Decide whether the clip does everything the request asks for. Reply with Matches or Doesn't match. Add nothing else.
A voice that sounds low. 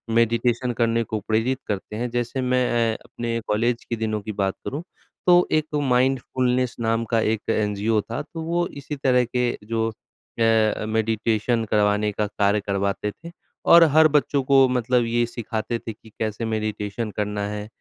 Matches